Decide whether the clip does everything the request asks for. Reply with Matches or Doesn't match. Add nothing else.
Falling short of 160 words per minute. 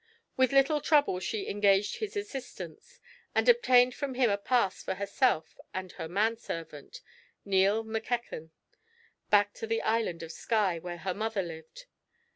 Matches